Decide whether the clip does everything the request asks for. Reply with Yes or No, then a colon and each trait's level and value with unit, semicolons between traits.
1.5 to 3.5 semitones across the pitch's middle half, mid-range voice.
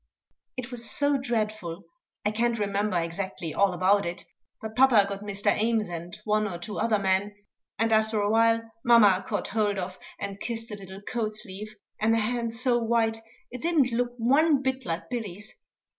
No: average, 2.9 semitones; high, 215 Hz